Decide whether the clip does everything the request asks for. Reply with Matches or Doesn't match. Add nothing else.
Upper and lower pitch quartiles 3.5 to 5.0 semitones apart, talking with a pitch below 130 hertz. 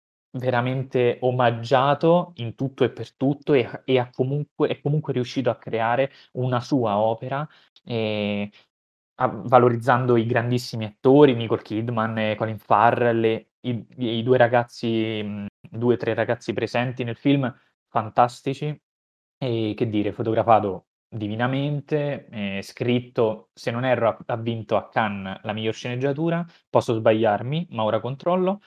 Doesn't match